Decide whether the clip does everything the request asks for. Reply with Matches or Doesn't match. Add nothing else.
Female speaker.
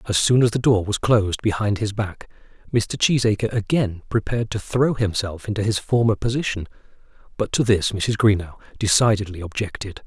Doesn't match